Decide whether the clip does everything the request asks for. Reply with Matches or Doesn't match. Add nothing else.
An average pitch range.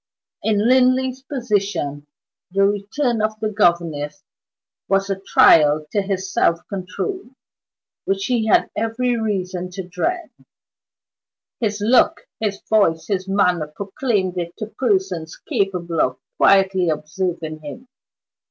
Matches